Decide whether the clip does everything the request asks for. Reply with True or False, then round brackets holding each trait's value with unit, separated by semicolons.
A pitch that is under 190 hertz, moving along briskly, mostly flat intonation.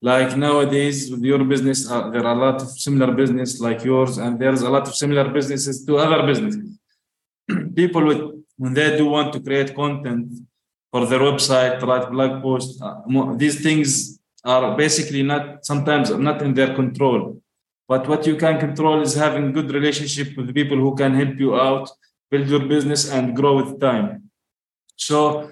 False (140 Hz; 175 wpm; 2.3 semitones)